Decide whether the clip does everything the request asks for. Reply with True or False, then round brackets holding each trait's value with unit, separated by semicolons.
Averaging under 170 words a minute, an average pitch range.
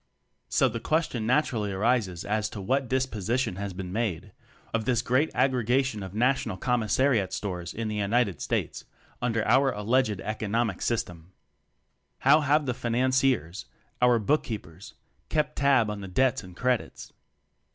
True (145 wpm; 4.4 semitones)